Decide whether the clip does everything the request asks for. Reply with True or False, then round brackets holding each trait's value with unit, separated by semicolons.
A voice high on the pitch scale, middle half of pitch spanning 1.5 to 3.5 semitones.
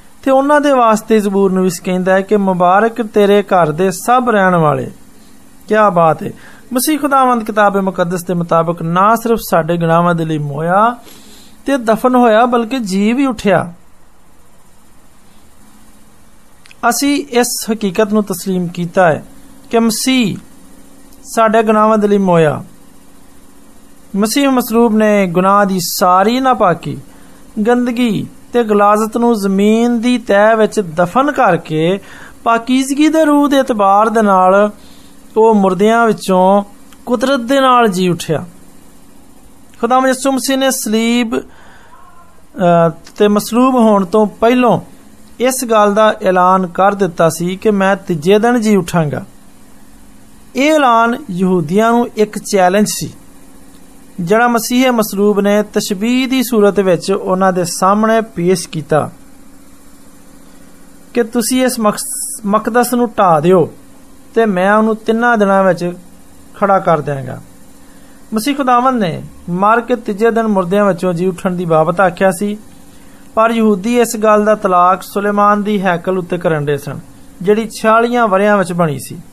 False (215 Hz; 4.5 semitones)